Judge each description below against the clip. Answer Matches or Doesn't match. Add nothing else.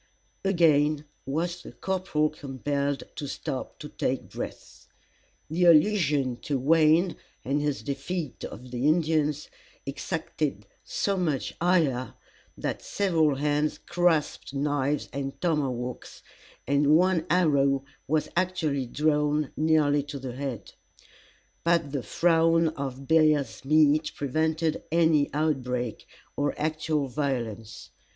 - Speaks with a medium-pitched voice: Matches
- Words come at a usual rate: Doesn't match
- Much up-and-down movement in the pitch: Doesn't match